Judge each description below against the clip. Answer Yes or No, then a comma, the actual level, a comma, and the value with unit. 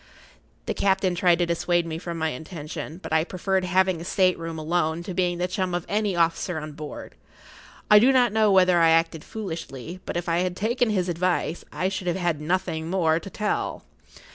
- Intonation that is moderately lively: No, narrow, 2.3 semitones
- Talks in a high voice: No, medium, 175 Hz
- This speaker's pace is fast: Yes, fast, 210 wpm